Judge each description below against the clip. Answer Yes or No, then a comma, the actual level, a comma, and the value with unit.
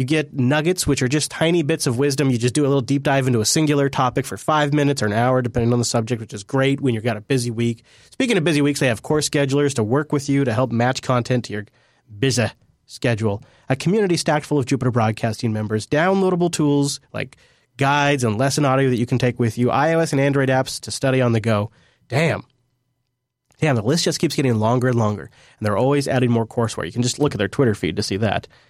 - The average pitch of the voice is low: Yes, low, 130 Hz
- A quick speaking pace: Yes, fast, 245 wpm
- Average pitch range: Yes, average, 3.2 semitones